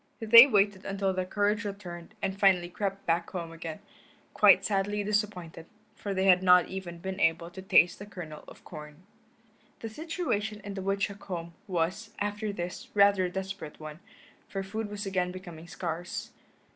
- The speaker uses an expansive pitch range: No, average, 2.8 semitones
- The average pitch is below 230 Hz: Yes, high, 190 Hz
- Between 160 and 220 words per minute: Yes, average, 170 wpm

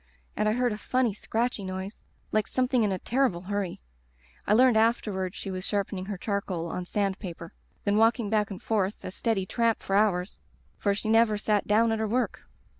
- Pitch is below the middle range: No, high, 210 Hz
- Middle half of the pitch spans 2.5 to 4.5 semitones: Yes, average, 2.9 semitones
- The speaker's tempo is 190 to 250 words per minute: Yes, average, 200 wpm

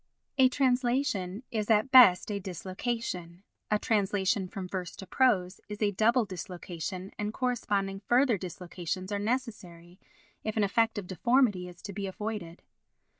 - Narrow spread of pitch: No, average, 3.8 semitones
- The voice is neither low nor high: No, high, 200 Hz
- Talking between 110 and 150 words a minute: Yes, average, 145 wpm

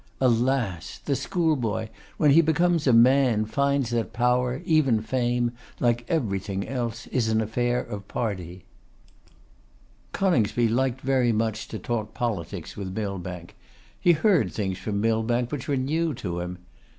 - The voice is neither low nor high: No, low, 120 Hz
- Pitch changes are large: No, average, 3.9 semitones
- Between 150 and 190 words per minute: No, average, 140 wpm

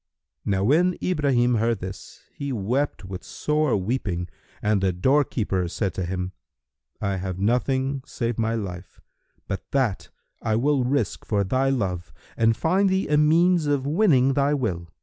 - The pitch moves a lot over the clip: Yes, wide, 6.6 semitones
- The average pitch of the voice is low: Yes, low, 120 Hz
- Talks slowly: No, average, 155 wpm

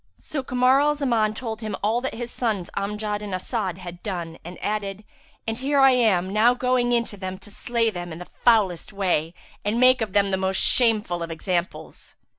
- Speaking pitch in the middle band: No, high, 210 Hz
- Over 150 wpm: Yes, fast, 205 wpm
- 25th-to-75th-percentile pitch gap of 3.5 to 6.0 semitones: Yes, average, 4.4 semitones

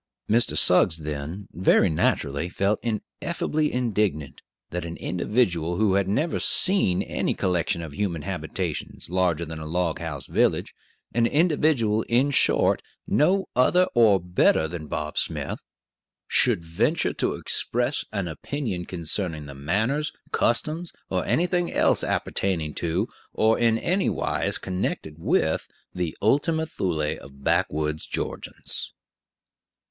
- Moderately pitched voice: No, very low, 95 Hz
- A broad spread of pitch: Yes, wide, 6.9 semitones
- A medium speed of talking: No, slow, 130 wpm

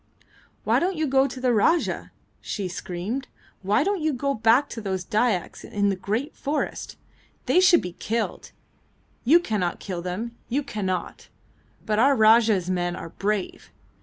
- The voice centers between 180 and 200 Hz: No, high, 220 Hz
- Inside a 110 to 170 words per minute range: Yes, average, 160 wpm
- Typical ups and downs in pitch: No, wide, 6.4 semitones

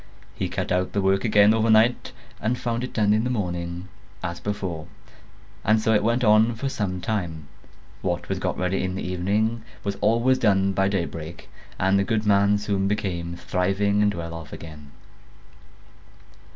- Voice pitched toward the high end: No, low, 100 Hz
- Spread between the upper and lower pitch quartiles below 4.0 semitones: Yes, average, 3.2 semitones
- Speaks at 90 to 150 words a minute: No, average, 170 wpm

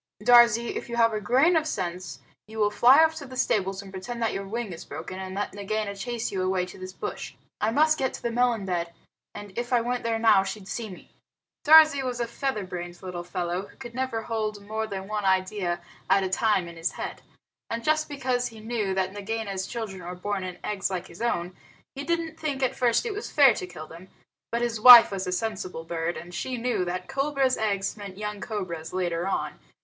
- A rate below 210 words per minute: No, fast, 225 wpm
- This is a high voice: Yes, high, 210 Hz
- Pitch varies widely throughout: No, average, 4.4 semitones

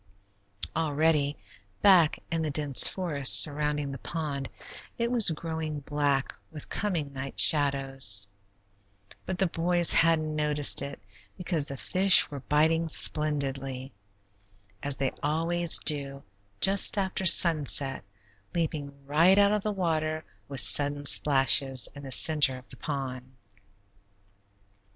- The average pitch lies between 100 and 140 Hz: No, medium, 150 Hz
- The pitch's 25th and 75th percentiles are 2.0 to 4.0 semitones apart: Yes, average, 3.0 semitones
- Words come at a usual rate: No, slow, 125 wpm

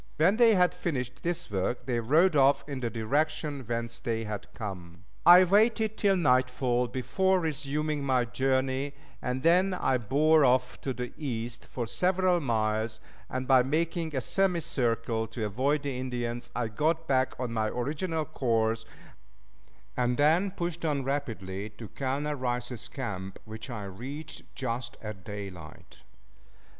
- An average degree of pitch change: Yes, average, 4.9 semitones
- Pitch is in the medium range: No, low, 130 Hz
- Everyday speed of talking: Yes, average, 150 wpm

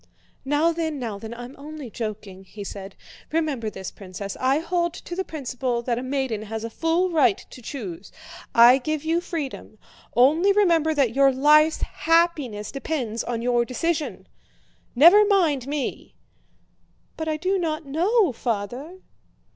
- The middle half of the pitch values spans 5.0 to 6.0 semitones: Yes, wide, 5.6 semitones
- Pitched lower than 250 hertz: No, very high, 275 Hz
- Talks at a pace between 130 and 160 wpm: Yes, average, 150 wpm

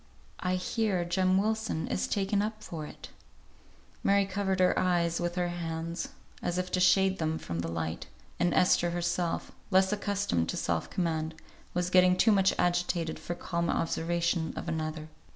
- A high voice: No, medium, 175 Hz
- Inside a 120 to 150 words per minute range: No, average, 165 wpm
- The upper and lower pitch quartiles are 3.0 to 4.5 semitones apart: No, narrow, 2.4 semitones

